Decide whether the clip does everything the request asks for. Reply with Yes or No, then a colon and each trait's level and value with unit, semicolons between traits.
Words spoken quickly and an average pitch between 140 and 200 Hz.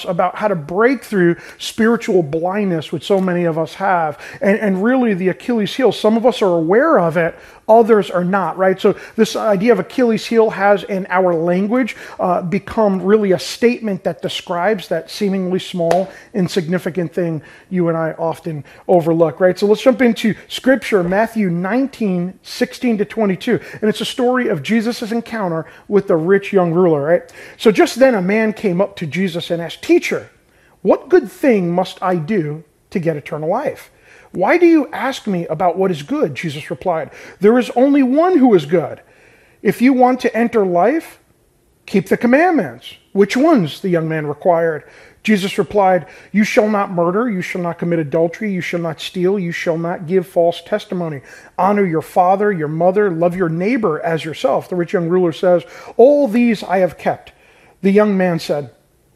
No: average, 185 wpm; high, 190 Hz